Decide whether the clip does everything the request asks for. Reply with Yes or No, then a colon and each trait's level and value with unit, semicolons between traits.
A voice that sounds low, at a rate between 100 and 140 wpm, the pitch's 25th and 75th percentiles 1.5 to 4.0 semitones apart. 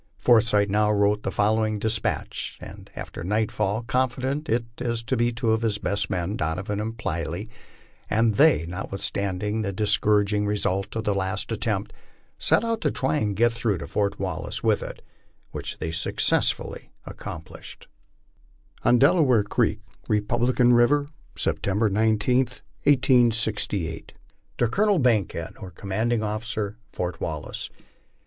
Yes: low, 110 Hz; slow, 135 wpm; average, 2.9 semitones